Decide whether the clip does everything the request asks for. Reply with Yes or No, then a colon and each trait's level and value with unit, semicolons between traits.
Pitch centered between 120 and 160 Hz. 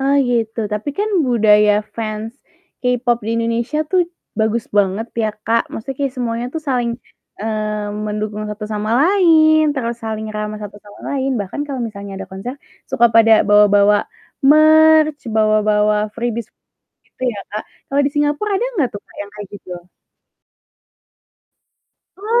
No: high, 225 Hz